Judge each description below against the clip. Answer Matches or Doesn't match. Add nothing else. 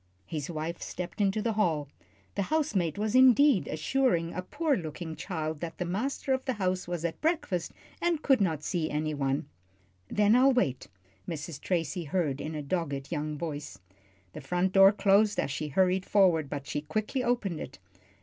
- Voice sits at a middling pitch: Matches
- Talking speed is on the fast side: Doesn't match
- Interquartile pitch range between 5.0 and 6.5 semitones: Matches